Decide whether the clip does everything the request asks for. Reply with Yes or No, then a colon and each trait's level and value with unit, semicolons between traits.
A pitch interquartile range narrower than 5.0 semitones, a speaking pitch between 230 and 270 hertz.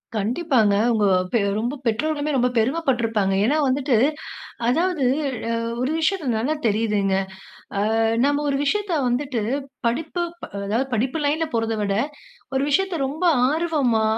No: wide, 5.5 semitones; very high, 260 Hz